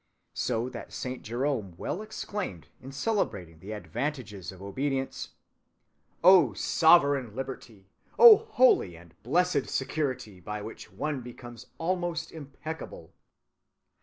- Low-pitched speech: Yes, low, 130 Hz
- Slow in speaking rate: Yes, slow, 110 wpm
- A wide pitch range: Yes, wide, 7.4 semitones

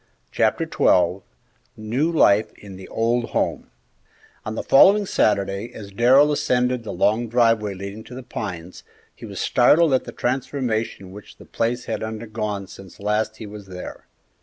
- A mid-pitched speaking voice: No, low, 110 Hz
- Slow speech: No, average, 160 wpm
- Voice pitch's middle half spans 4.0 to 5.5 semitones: No, average, 3.6 semitones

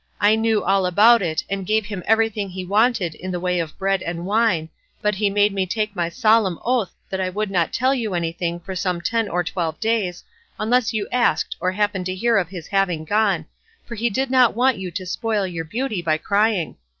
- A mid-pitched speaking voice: No, high, 195 Hz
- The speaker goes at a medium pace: No, fast, 220 wpm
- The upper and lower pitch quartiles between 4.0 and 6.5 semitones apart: No, average, 3.6 semitones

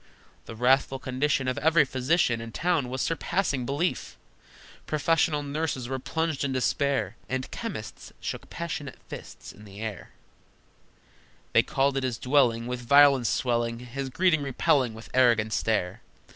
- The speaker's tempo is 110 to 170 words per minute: Yes, average, 145 wpm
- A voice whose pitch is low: Yes, low, 130 Hz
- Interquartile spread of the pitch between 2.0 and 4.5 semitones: Yes, average, 3.6 semitones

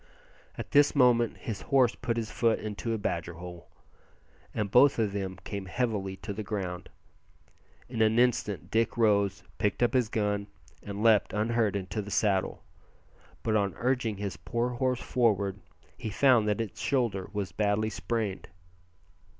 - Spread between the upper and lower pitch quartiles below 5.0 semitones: Yes, average, 2.8 semitones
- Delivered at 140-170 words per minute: Yes, average, 160 wpm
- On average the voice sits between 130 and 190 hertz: No, low, 110 Hz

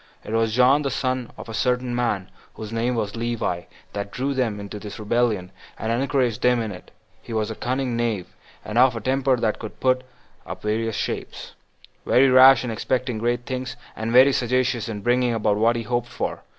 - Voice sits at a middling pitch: No, low, 120 Hz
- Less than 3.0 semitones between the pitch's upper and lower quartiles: Yes, narrow, 2.6 semitones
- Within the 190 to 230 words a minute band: Yes, average, 200 wpm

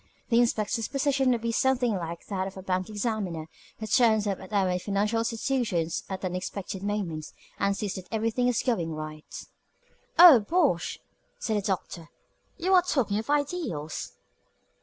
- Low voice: No, high, 210 Hz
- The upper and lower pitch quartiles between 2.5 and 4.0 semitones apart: No, average, 4.7 semitones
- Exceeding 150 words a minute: Yes, average, 160 wpm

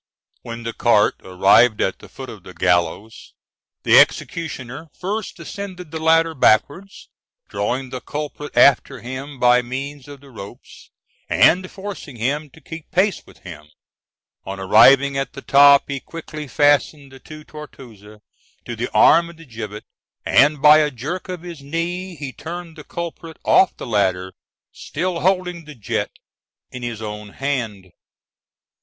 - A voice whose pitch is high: No, medium, 140 Hz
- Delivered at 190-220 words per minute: No, average, 155 wpm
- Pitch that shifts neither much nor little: No, wide, 5.9 semitones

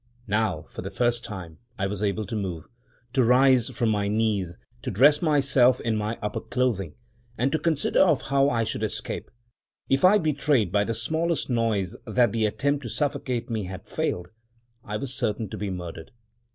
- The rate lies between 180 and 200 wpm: Yes, average, 195 wpm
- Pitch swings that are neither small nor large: Yes, average, 4.5 semitones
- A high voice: No, low, 115 Hz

